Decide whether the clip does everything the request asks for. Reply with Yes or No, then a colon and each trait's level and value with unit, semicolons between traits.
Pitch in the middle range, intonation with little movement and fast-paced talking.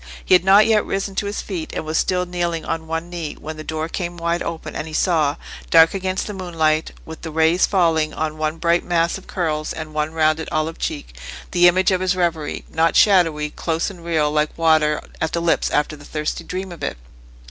Yes: medium, 165 Hz; narrow, 2.3 semitones; fast, 215 wpm